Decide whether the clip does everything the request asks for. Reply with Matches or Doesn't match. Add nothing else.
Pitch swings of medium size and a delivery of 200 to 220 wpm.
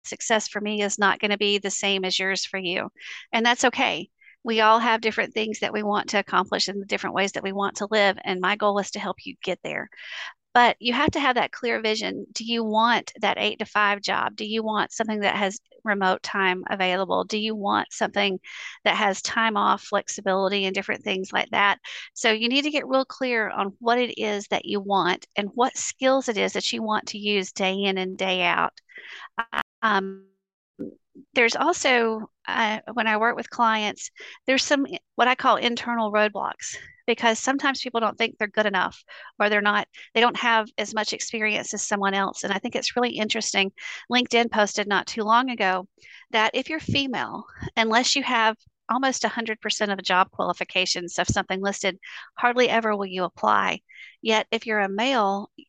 Matches